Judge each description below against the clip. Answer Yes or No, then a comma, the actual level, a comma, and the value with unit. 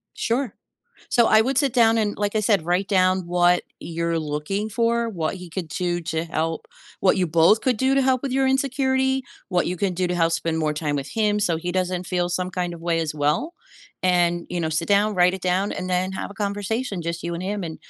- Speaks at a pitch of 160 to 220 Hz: Yes, medium, 185 Hz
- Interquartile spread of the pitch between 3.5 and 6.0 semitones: Yes, average, 4.3 semitones